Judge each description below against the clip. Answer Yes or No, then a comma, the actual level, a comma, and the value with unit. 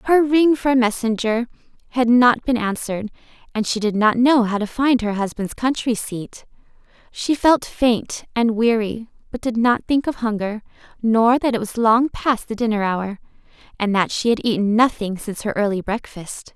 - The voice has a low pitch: No, high, 230 Hz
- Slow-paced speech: No, average, 185 wpm